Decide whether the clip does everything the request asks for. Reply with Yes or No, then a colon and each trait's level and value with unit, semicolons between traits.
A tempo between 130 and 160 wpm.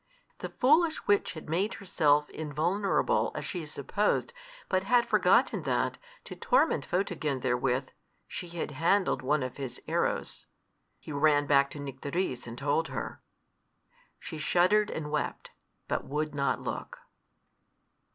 Yes: slow, 135 wpm